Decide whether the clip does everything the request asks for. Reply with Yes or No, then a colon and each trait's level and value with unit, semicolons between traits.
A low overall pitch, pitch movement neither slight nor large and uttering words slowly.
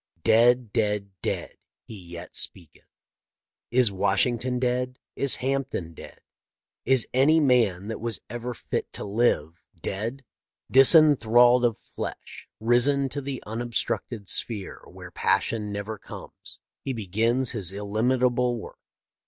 Yes: low, 120 Hz; average, 3.5 semitones; slow, 120 wpm